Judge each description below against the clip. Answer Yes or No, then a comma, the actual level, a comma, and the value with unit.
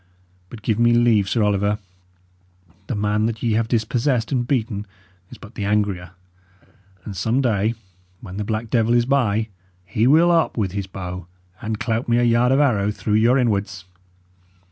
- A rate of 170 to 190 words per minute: Yes, average, 175 wpm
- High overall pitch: No, low, 110 Hz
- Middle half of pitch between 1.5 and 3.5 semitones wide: Yes, average, 2.7 semitones